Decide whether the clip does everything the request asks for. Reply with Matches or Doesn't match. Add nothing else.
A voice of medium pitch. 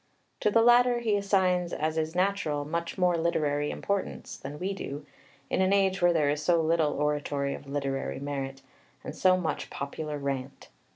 Matches